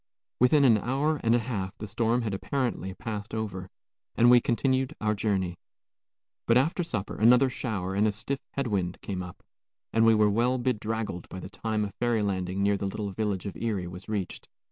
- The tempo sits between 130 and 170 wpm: No, average, 195 wpm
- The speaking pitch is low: Yes, low, 110 Hz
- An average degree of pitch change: Yes, average, 3.5 semitones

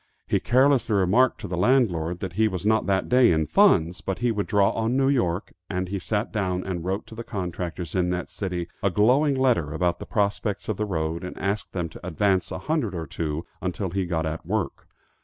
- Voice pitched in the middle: No, very low, 95 Hz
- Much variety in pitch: No, average, 4.0 semitones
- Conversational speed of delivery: No, fast, 220 wpm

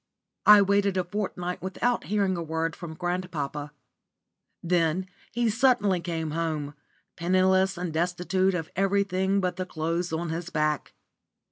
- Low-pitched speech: No, medium, 180 Hz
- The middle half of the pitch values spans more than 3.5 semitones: No, average, 2.7 semitones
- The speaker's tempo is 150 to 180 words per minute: No, slow, 135 wpm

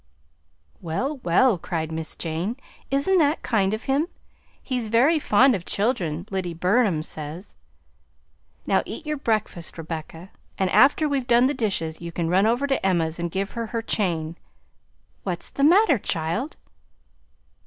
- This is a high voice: Yes, high, 205 Hz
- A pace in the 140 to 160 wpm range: Yes, average, 150 wpm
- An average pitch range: No, wide, 7.7 semitones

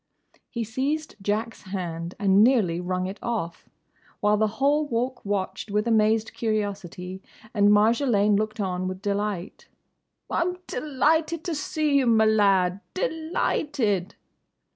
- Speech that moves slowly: Yes, slow, 125 wpm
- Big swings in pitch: No, average, 5.0 semitones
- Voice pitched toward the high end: Yes, high, 215 Hz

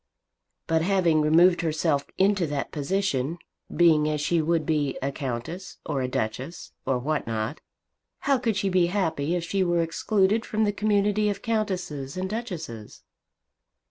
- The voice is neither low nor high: Yes, medium, 170 Hz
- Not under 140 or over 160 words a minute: Yes, average, 155 wpm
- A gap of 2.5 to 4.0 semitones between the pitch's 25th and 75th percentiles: No, average, 5.1 semitones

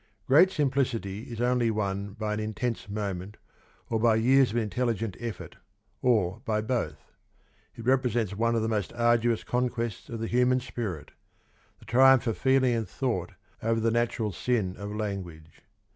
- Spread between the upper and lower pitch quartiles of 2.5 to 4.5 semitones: Yes, average, 2.9 semitones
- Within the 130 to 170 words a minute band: Yes, average, 160 wpm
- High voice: No, low, 115 Hz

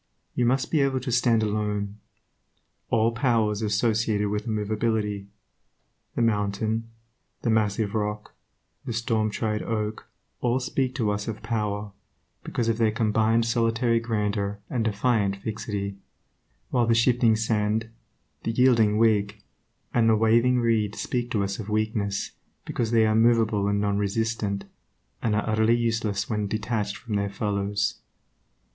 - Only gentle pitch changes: Yes, narrow, 1.8 semitones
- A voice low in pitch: Yes, low, 110 Hz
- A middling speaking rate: Yes, average, 145 wpm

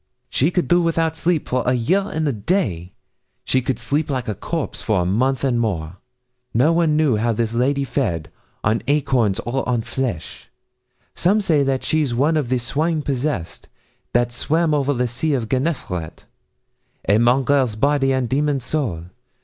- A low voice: Yes, low, 130 Hz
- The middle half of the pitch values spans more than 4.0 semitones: Yes, average, 4.4 semitones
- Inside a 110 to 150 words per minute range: No, average, 175 wpm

